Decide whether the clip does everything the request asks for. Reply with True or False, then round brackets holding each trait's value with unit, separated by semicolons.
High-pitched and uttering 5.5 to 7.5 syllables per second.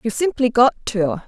True (235 Hz; 5.7 syllables/s)